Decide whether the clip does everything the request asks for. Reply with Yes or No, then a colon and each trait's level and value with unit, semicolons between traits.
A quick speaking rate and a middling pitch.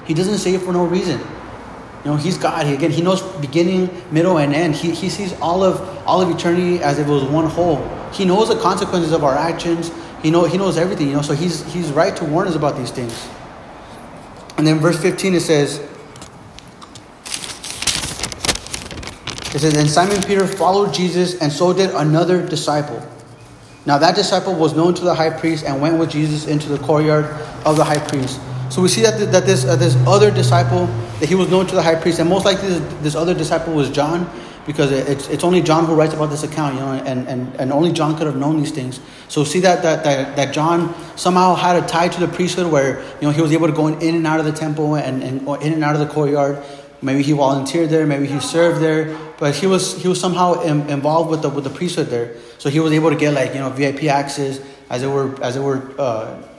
Yes: fast, 240 wpm; medium, 155 Hz